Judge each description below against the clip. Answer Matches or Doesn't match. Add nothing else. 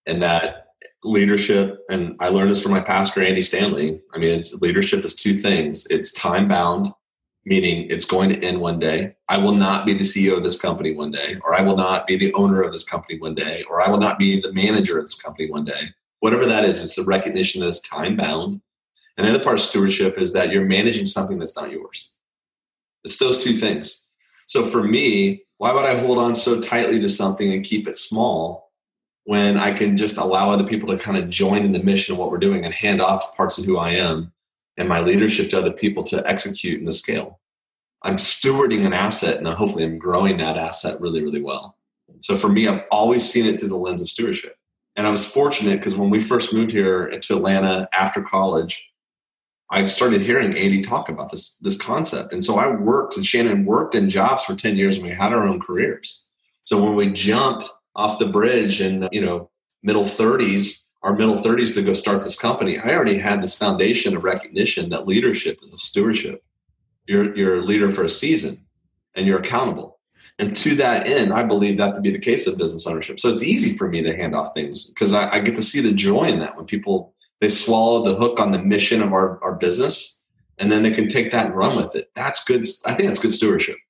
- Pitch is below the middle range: Matches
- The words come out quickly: Matches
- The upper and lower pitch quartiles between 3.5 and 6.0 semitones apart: Matches